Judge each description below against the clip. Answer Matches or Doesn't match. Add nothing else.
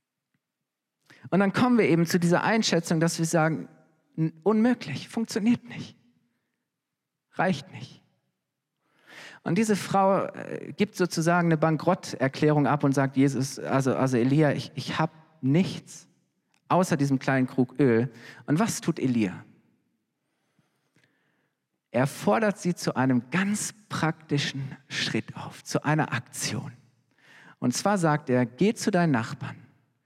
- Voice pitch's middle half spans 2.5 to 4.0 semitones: Doesn't match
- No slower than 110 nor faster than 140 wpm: Matches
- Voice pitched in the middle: Matches